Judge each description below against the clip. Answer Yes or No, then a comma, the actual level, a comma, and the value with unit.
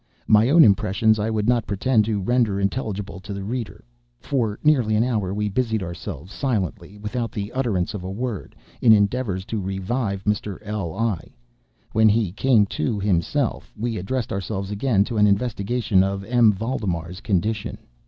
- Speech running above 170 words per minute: No, average, 155 wpm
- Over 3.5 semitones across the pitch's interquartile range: No, average, 3.1 semitones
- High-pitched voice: No, low, 105 Hz